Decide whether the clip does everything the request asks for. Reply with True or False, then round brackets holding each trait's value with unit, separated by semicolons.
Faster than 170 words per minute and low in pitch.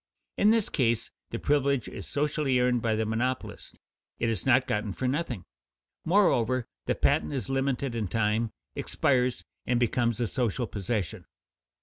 False (150 wpm; 125 Hz)